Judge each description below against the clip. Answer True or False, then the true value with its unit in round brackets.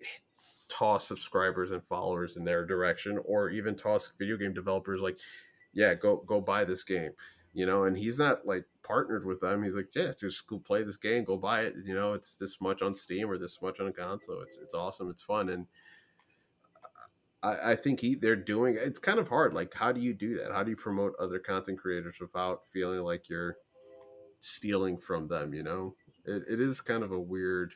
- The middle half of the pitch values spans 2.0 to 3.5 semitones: True (2.9 semitones)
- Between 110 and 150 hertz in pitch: False (95 Hz)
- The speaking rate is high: True (210 wpm)